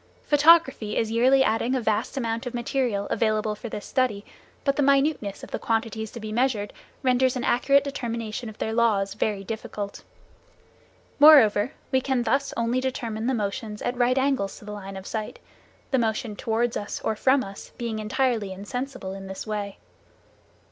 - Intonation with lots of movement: No, average, 3.6 semitones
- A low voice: No, high, 230 Hz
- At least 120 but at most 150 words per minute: No, average, 175 wpm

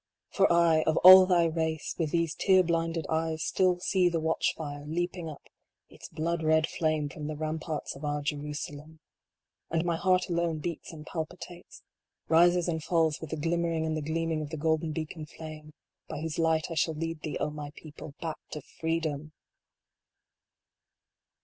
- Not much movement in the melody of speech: Yes, narrow, 1.6 semitones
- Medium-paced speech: Yes, average, 175 wpm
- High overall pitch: No, medium, 160 Hz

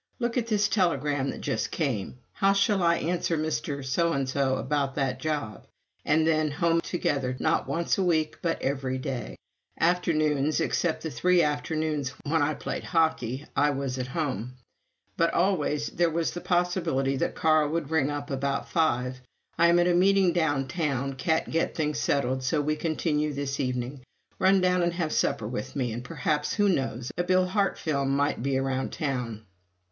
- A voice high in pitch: No, medium, 150 Hz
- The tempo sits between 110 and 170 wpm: No, average, 180 wpm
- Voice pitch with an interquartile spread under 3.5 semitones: No, average, 3.9 semitones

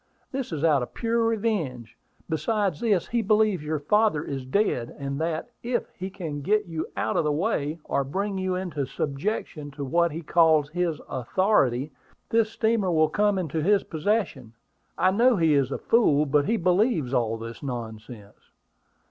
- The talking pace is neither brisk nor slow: Yes, average, 175 wpm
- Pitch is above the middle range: No, medium, 165 Hz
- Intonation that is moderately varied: No, wide, 6.7 semitones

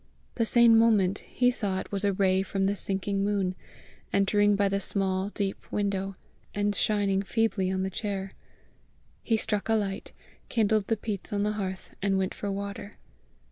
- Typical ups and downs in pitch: No, narrow, 1.4 semitones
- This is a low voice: No, high, 200 Hz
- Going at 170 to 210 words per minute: Yes, average, 175 wpm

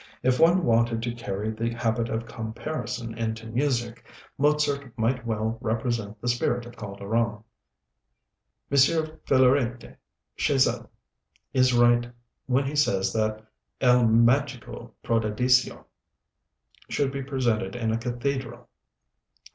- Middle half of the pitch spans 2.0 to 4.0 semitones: Yes, narrow, 2.5 semitones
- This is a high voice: No, low, 120 Hz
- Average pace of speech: No, slow, 115 wpm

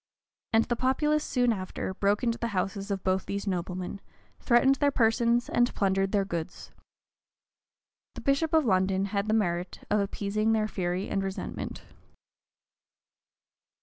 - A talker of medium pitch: No, high, 205 Hz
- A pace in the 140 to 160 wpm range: Yes, average, 150 wpm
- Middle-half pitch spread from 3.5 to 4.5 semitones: Yes, average, 3.8 semitones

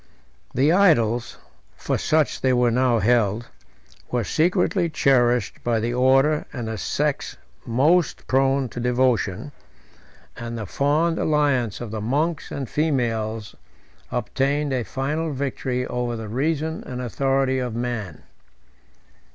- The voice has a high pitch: No, low, 125 Hz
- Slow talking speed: Yes, slow, 125 wpm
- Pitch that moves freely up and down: No, average, 3.4 semitones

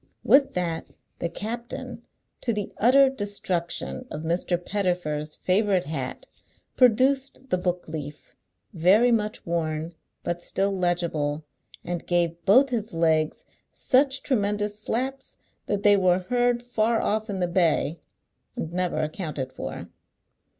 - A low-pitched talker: No, medium, 185 Hz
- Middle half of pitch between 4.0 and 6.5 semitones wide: Yes, average, 5.2 semitones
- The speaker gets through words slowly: Yes, slow, 130 wpm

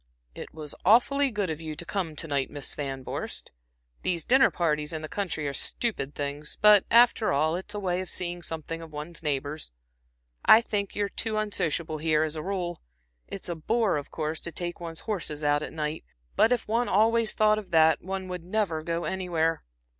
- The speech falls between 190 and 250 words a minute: Yes, average, 200 wpm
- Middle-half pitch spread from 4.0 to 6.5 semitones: Yes, average, 4.8 semitones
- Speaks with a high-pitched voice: No, medium, 170 Hz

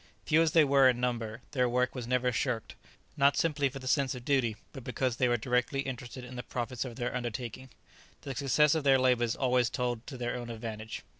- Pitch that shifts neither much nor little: No, narrow, 2.0 semitones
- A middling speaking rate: No, fast, 220 wpm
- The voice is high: No, low, 125 Hz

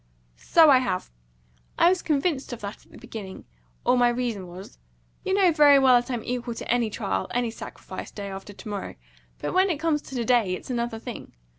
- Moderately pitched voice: No, high, 245 Hz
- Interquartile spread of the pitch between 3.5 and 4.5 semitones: No, average, 5.1 semitones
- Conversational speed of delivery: No, fast, 210 wpm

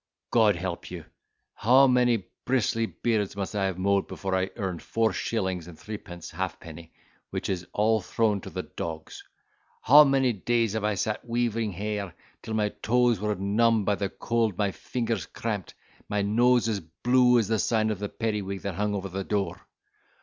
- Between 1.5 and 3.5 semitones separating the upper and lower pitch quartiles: Yes, average, 3.0 semitones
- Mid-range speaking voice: No, low, 105 Hz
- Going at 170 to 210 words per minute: Yes, average, 180 wpm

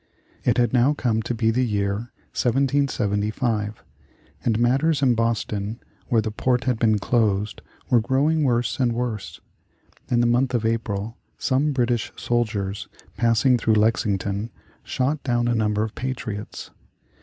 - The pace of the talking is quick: No, average, 145 wpm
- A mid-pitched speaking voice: No, low, 115 Hz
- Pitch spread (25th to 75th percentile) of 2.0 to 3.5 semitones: Yes, average, 2.8 semitones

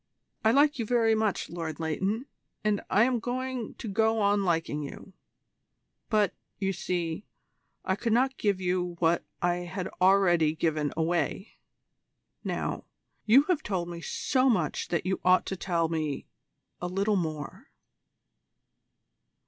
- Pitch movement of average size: Yes, average, 4.5 semitones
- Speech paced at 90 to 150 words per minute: Yes, average, 140 wpm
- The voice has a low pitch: No, high, 190 Hz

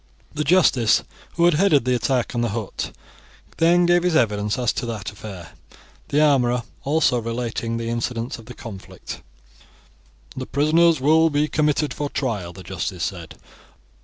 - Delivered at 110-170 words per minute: Yes, average, 160 wpm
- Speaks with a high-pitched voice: No, low, 125 Hz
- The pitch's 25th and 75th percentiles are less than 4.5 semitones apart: No, average, 4.9 semitones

